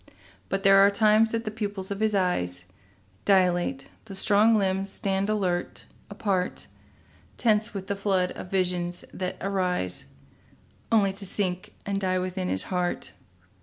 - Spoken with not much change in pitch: Yes, narrow, 2.1 semitones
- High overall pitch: Yes, high, 195 Hz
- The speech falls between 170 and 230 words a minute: No, average, 140 wpm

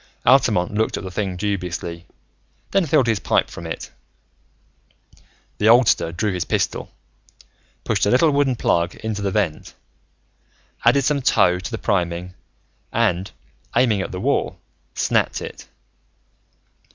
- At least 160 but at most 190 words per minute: No, slow, 135 wpm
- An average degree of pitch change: Yes, average, 4.8 semitones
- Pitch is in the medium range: No, low, 100 Hz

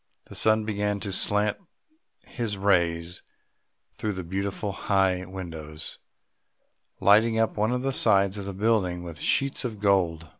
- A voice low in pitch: Yes, low, 100 Hz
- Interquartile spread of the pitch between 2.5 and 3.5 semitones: Yes, average, 2.9 semitones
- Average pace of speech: Yes, average, 145 wpm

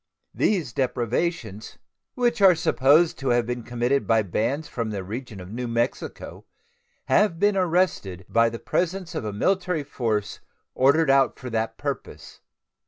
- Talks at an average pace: Yes, average, 150 wpm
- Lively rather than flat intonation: Yes, wide, 6.7 semitones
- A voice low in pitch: Yes, low, 125 Hz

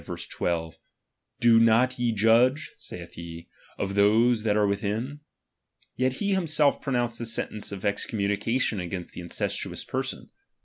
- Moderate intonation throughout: Yes, average, 3.6 semitones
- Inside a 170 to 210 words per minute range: No, average, 140 wpm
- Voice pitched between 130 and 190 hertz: No, low, 110 Hz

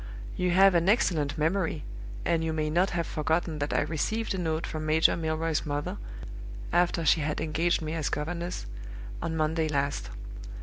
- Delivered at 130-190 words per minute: Yes, average, 170 wpm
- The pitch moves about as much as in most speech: No, narrow, 2.1 semitones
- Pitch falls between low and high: Yes, medium, 160 Hz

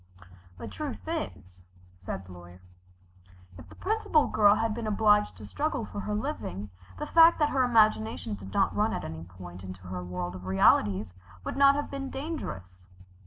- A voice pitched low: Yes, low, 100 Hz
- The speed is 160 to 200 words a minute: Yes, average, 175 wpm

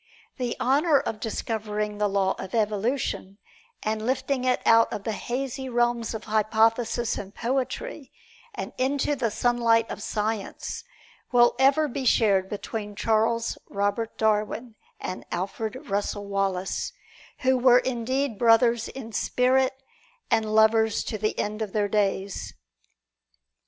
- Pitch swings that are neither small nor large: Yes, average, 3.1 semitones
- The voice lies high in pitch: Yes, high, 225 Hz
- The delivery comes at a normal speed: No, slow, 130 wpm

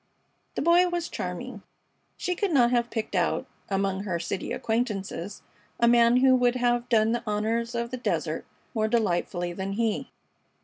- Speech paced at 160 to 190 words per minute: Yes, average, 165 wpm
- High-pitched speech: Yes, high, 235 Hz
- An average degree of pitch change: Yes, average, 3.7 semitones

